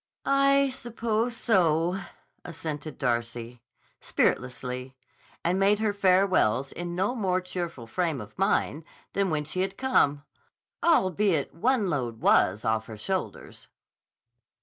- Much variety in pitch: Yes, wide, 7.1 semitones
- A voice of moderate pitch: Yes, medium, 175 Hz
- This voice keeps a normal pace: No, slow, 120 wpm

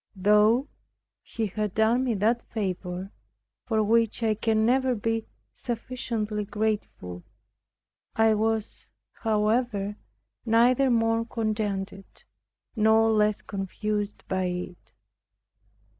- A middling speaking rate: No, slow, 100 wpm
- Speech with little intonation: Yes, narrow, 1.8 semitones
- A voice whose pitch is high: Yes, high, 215 Hz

